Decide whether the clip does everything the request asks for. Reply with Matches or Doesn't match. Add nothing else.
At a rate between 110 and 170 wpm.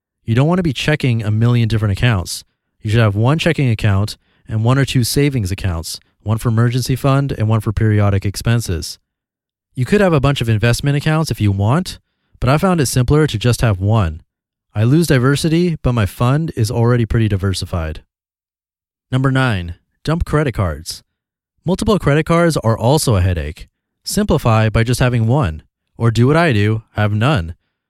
Doesn't match